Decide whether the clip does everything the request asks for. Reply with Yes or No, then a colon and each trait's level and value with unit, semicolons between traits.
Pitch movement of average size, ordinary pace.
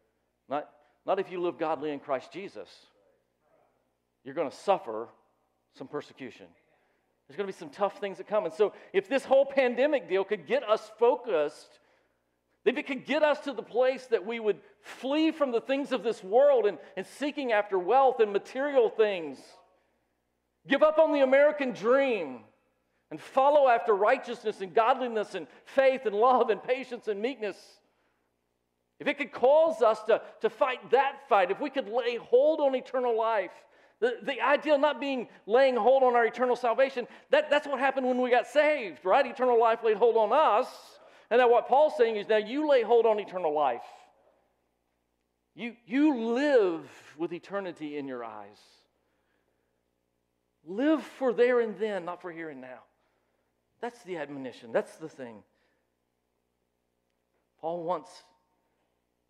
No: wide, 8.8 semitones; average, 165 wpm